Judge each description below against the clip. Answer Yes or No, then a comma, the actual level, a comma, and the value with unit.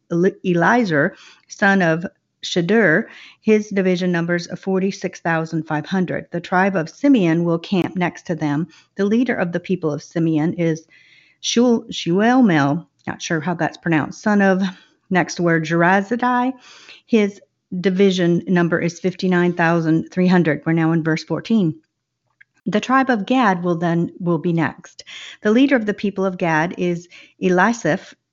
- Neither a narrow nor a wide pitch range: Yes, average, 3.1 semitones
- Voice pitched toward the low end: No, medium, 180 Hz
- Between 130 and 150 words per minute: Yes, average, 140 wpm